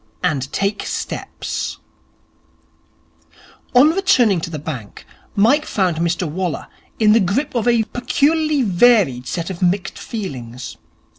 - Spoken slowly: Yes, slow, 125 wpm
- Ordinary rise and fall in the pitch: No, wide, 6.6 semitones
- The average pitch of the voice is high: Yes, high, 195 Hz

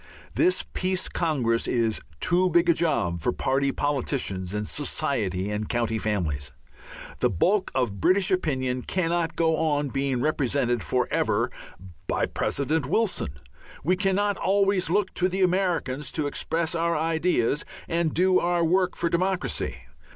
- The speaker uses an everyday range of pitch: No, wide, 6.7 semitones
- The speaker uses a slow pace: No, average, 145 wpm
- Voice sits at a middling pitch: Yes, medium, 160 Hz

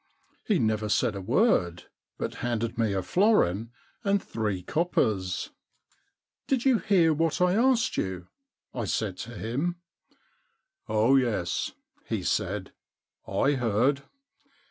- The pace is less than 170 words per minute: Yes, average, 145 wpm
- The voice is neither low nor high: No, low, 120 Hz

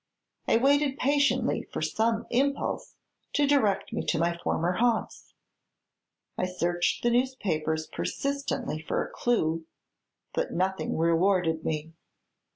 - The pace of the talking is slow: Yes, slow, 120 wpm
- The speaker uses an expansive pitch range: Yes, wide, 7.6 semitones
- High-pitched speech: Yes, high, 195 Hz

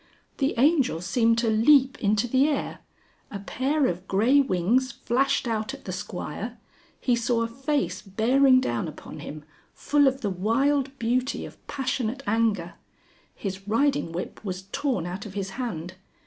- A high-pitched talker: Yes, high, 230 Hz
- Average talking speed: Yes, average, 160 wpm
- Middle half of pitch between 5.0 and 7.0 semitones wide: Yes, wide, 5.5 semitones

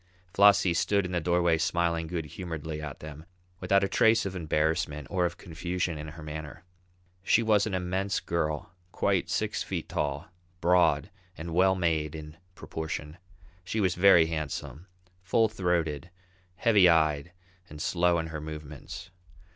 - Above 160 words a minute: No, average, 150 wpm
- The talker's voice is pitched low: Yes, very low, 85 Hz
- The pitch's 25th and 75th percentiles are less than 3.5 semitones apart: Yes, average, 2.9 semitones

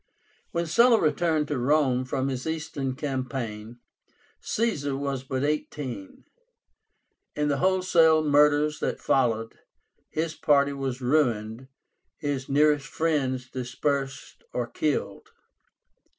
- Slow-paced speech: Yes, slow, 110 wpm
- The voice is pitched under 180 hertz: Yes, medium, 140 Hz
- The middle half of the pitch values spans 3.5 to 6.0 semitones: No, average, 2.9 semitones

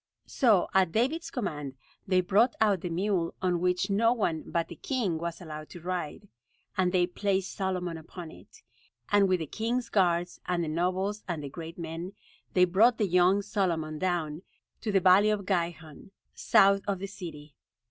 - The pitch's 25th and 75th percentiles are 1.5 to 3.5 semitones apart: Yes, average, 3.1 semitones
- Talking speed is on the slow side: No, average, 180 wpm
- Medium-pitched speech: Yes, medium, 180 Hz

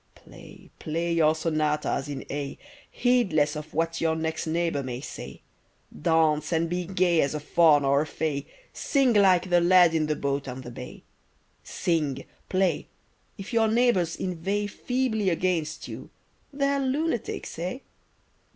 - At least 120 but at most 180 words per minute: Yes, average, 145 wpm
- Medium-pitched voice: Yes, medium, 165 Hz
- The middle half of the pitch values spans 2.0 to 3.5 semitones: No, average, 4.0 semitones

